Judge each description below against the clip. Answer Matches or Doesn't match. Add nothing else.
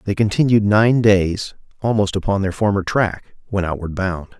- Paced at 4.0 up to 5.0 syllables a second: Matches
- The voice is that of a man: Matches